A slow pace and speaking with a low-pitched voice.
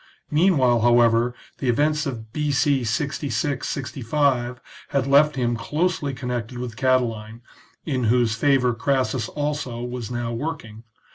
Yes: slow, 125 wpm; low, 125 Hz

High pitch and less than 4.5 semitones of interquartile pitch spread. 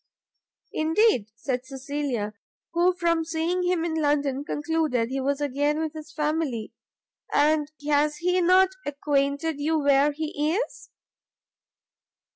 Yes: very high, 300 Hz; narrow, 2.4 semitones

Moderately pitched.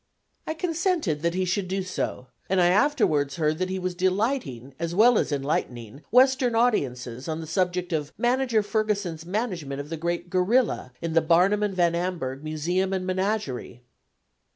Yes: medium, 180 Hz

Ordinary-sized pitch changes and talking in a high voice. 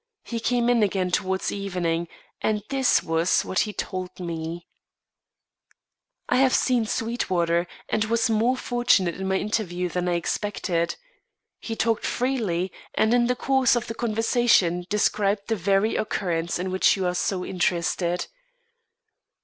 Yes: average, 4.3 semitones; high, 195 Hz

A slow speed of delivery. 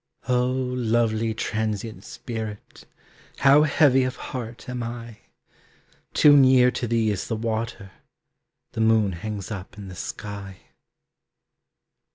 Yes: slow, 120 wpm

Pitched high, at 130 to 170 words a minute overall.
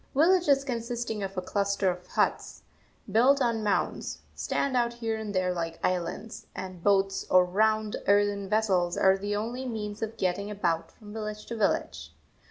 Yes: high, 205 Hz; average, 165 wpm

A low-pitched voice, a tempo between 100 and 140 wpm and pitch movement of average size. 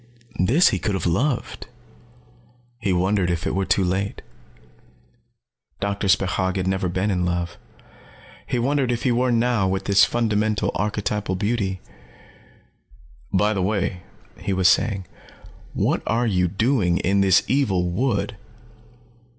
Yes: low, 100 Hz; slow, 135 wpm; average, 3.4 semitones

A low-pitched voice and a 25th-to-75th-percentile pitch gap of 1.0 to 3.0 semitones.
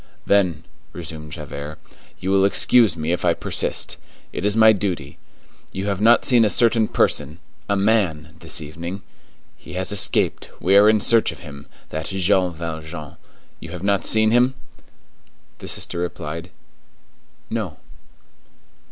No: very low, 90 Hz; average, 4.2 semitones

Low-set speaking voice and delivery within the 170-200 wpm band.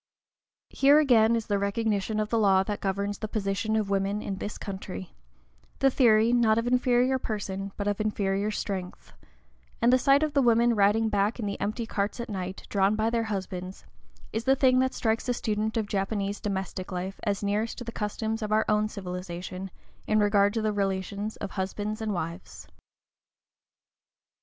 No: high, 210 Hz; average, 180 wpm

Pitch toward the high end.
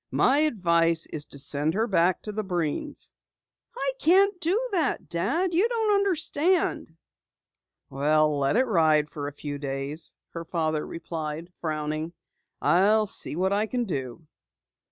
No: medium, 170 Hz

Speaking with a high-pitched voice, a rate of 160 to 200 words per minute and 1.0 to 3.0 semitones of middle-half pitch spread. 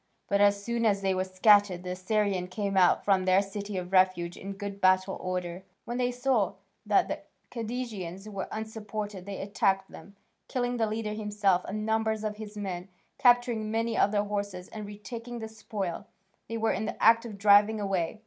Yes: high, 205 Hz; average, 185 wpm; narrow, 2.5 semitones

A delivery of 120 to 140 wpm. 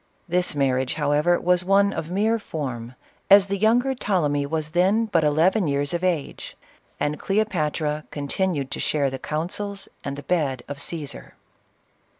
No: average, 155 wpm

